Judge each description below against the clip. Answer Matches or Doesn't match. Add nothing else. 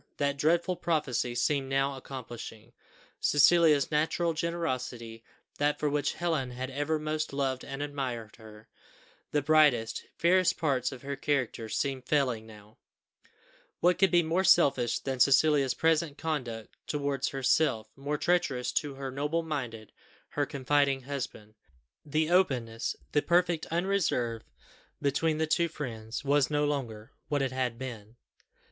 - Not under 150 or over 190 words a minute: Doesn't match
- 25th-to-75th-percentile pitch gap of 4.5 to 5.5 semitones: Doesn't match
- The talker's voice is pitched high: Doesn't match